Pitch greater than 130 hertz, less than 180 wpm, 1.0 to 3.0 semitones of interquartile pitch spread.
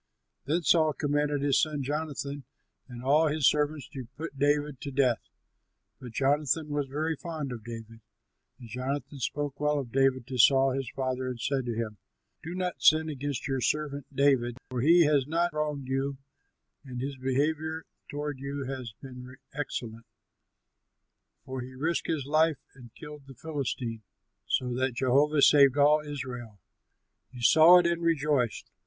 Yes: medium, 140 Hz; average, 160 wpm; average, 2.7 semitones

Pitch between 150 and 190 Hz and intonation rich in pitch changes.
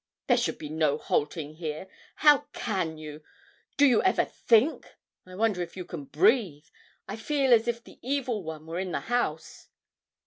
Yes: medium, 185 Hz; wide, 7.4 semitones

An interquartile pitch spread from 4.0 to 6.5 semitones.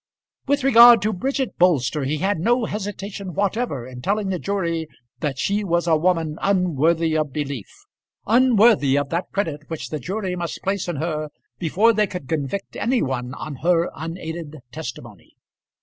Yes: average, 4.8 semitones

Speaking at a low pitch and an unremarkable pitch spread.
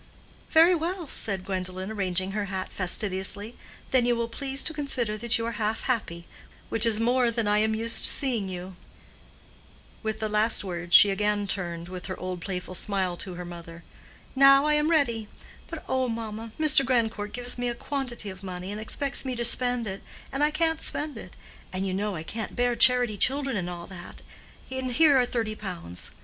No: high, 220 Hz; average, 4.9 semitones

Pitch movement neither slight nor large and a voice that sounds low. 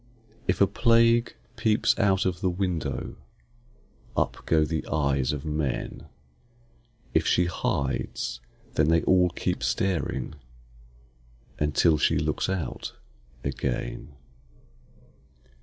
Yes: average, 4.3 semitones; very low, 85 Hz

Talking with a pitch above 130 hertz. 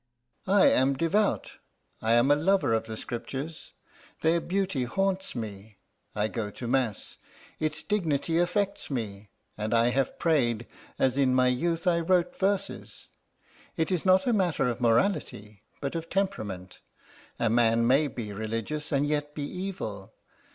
Yes: medium, 140 Hz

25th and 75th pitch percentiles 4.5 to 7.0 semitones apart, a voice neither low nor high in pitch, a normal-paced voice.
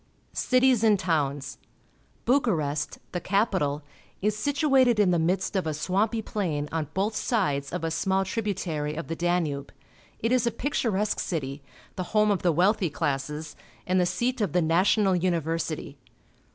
Yes: average, 5.2 semitones; medium, 180 Hz; average, 160 wpm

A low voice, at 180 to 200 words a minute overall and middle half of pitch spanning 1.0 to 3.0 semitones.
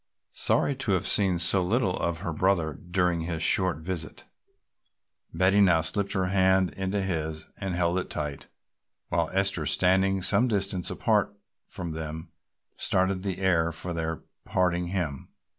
No: very low, 90 Hz; average, 150 wpm; narrow, 2.5 semitones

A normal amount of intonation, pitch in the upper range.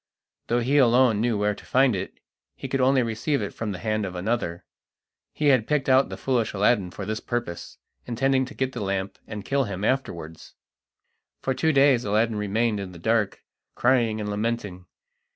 No: average, 4.1 semitones; low, 115 Hz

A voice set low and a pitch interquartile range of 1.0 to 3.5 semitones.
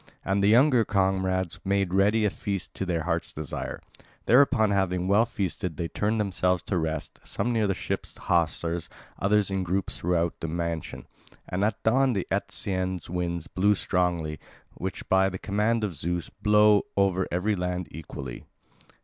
Yes: very low, 95 Hz; average, 2.9 semitones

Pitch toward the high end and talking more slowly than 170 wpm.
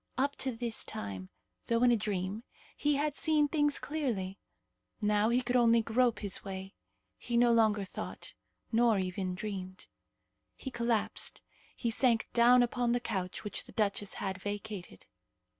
Yes: high, 225 Hz; average, 155 wpm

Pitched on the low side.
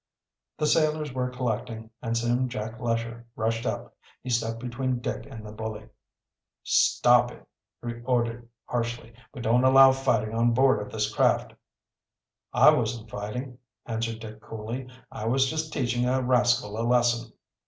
Yes: low, 120 Hz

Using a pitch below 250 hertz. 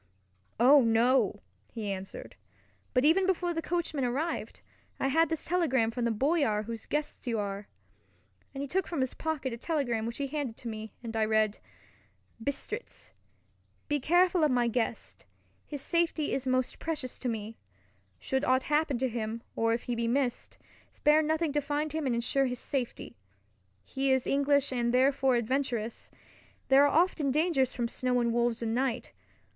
No: very high, 260 Hz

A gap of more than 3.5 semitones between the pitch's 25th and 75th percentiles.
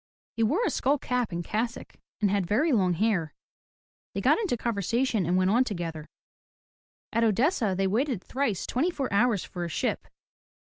Yes: average, 5.1 semitones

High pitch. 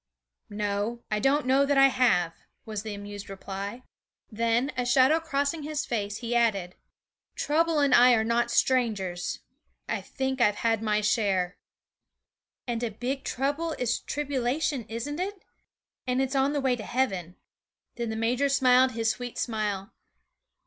Yes: high, 240 Hz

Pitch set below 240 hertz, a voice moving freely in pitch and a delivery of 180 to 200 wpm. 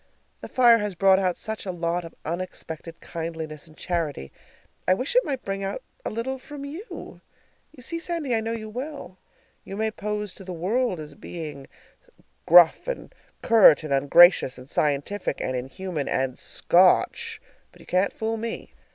Yes: high, 190 Hz; wide, 6.0 semitones; average, 185 wpm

